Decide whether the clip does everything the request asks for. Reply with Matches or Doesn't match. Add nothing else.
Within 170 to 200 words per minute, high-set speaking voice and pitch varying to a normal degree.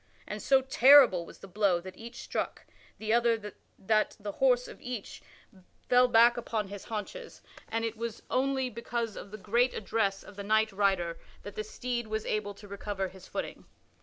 Matches